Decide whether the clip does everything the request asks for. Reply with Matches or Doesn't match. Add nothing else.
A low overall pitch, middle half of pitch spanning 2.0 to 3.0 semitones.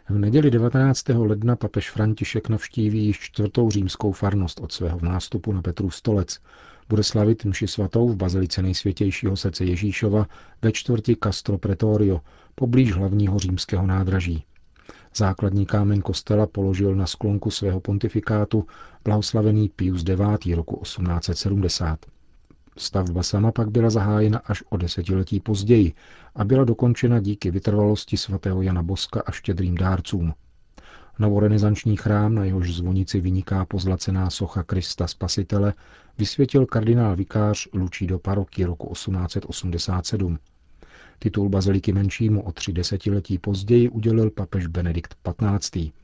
Matches